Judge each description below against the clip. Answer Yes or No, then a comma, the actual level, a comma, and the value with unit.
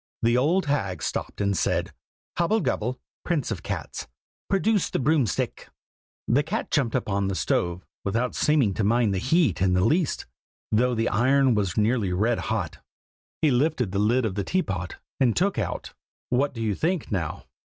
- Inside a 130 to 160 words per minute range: No, average, 180 wpm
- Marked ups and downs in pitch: Yes, wide, 6.4 semitones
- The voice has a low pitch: Yes, low, 120 Hz